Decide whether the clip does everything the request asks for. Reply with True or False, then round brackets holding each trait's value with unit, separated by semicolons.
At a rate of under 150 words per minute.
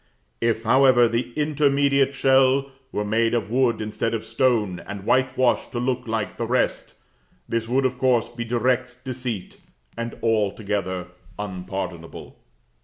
True (135 wpm)